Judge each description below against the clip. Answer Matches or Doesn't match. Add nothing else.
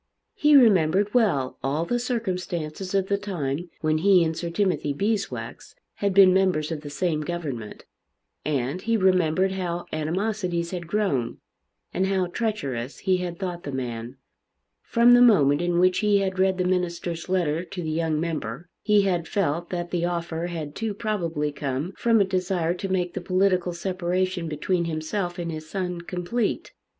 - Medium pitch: Matches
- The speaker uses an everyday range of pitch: Matches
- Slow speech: Doesn't match